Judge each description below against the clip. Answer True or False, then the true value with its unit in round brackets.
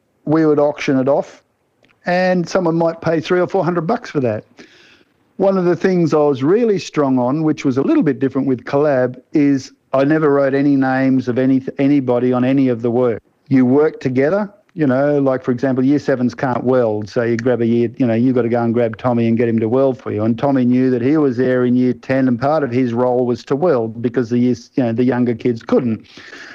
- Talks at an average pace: False (240 wpm)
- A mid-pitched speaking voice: False (130 Hz)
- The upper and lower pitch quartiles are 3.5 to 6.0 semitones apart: False (3.0 semitones)